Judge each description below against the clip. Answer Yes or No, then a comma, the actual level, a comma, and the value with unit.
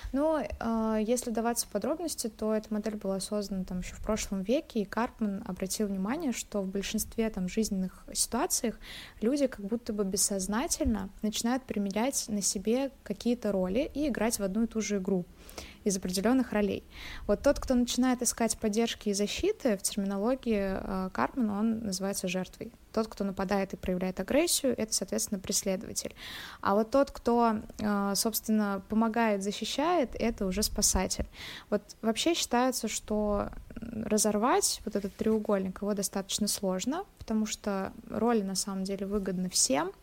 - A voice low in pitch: No, high, 215 Hz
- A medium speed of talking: Yes, average, 150 wpm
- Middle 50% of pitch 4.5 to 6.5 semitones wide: No, average, 2.8 semitones